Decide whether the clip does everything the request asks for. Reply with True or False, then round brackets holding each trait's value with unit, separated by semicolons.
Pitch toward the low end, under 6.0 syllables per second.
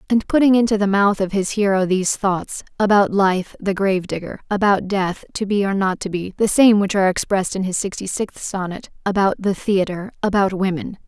False (195 Hz; 4.9 syllables/s)